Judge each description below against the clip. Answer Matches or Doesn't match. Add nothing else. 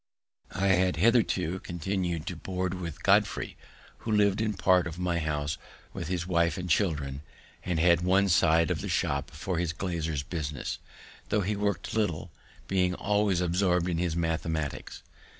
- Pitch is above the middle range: Doesn't match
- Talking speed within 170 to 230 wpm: Doesn't match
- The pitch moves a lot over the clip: Doesn't match